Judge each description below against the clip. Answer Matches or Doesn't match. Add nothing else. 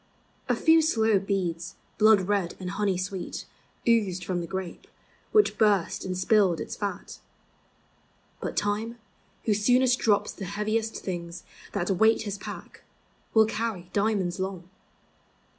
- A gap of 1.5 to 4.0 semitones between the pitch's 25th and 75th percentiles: Matches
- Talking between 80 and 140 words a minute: Matches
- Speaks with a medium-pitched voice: Doesn't match